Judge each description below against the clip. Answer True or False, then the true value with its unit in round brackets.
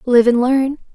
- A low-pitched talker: False (255 Hz)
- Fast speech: False (190 wpm)